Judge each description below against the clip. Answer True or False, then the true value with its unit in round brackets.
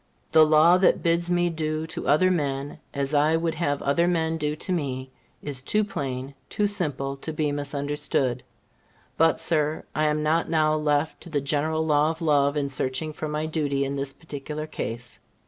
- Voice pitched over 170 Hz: False (150 Hz)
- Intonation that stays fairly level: True (2.3 semitones)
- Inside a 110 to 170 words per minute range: False (185 wpm)